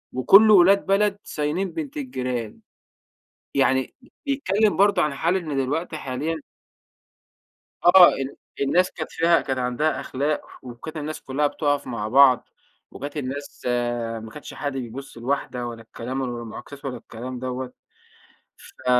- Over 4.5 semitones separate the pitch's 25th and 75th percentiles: Yes, average, 5.1 semitones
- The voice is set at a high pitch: No, medium, 140 Hz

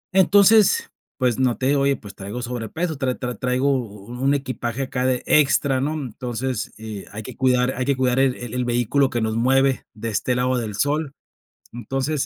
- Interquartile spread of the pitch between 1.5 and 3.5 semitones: Yes, narrow, 2.4 semitones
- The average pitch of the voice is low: Yes, low, 130 Hz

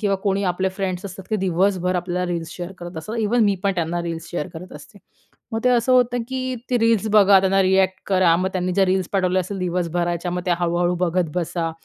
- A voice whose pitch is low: No, medium, 185 Hz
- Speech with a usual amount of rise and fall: No, narrow, 2.3 semitones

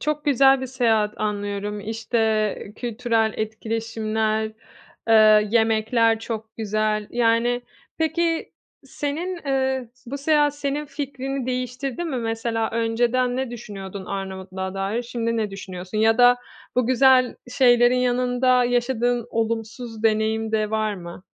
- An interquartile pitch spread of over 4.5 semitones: No, average, 2.7 semitones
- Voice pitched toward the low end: No, high, 230 Hz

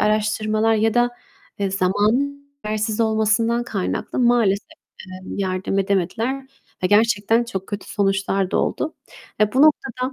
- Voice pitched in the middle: No, high, 215 Hz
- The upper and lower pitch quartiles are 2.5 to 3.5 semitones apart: Yes, average, 3.2 semitones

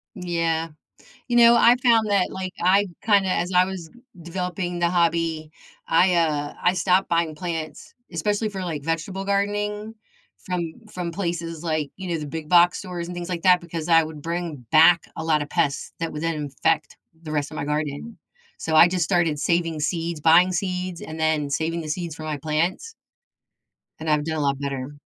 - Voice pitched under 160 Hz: No, medium, 170 Hz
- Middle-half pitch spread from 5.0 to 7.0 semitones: No, average, 2.7 semitones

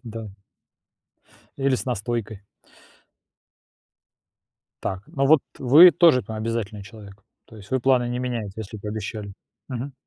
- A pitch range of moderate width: Yes, average, 3.5 semitones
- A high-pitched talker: No, low, 115 Hz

